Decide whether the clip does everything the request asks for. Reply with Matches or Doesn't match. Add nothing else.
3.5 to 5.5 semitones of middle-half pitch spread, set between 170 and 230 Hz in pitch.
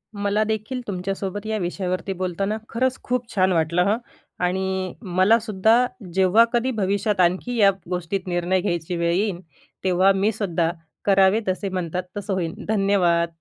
Doesn't match